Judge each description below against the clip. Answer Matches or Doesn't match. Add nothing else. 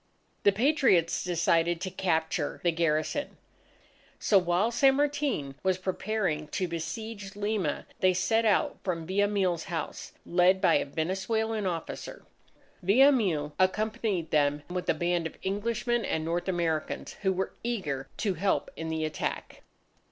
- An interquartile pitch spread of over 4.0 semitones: Matches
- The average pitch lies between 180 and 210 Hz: Matches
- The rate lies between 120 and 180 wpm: Matches